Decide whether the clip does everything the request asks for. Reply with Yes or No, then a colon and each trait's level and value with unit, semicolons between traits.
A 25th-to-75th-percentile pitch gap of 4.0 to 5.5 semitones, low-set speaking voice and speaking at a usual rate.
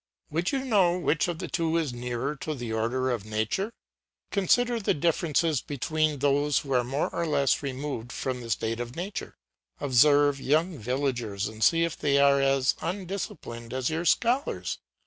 No: average, 5.1 semitones; medium, 145 Hz; average, 170 wpm